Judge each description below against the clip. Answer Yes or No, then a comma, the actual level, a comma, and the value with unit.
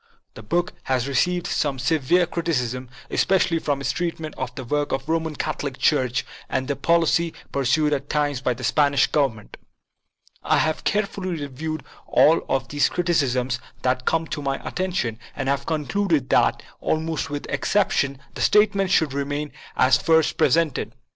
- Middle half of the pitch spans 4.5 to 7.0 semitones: No, average, 3.8 semitones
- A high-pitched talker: No, medium, 145 Hz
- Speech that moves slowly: No, average, 165 wpm